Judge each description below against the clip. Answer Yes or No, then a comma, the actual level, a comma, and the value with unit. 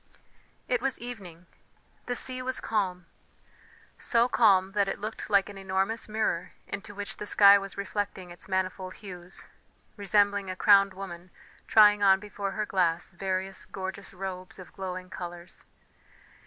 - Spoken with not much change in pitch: Yes, narrow, 1.9 semitones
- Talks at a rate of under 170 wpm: Yes, average, 145 wpm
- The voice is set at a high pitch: Yes, high, 195 Hz